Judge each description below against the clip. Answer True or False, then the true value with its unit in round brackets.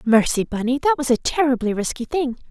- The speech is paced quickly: False (190 wpm)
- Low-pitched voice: False (255 Hz)